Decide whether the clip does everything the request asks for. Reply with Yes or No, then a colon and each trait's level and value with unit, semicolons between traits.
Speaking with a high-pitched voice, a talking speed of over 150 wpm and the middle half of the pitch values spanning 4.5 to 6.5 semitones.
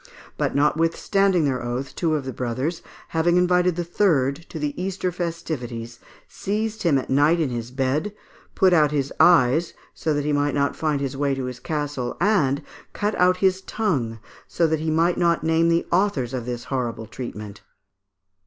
No: medium, 150 Hz; average, 180 wpm; average, 4.9 semitones